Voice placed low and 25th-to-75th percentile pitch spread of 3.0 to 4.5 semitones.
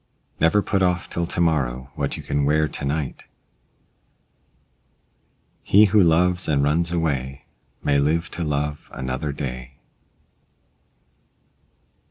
Yes: very low, 75 Hz; average, 3.5 semitones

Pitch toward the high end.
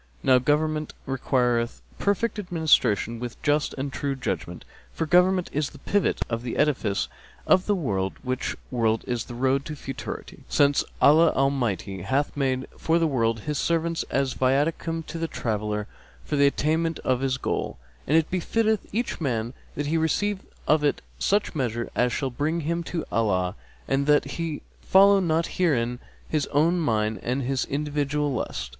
No: medium, 140 Hz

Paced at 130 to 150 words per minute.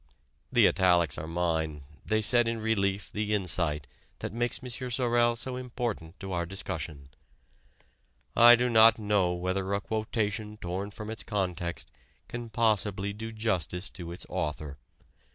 Yes: average, 145 wpm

